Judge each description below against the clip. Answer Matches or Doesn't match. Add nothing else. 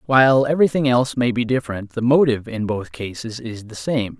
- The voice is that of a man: Matches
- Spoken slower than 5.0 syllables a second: Doesn't match